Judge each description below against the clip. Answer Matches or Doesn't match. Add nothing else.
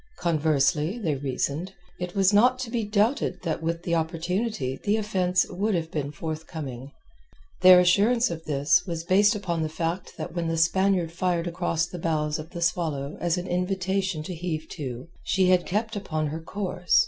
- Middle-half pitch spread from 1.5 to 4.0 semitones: Matches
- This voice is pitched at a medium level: Matches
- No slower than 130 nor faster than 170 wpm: Doesn't match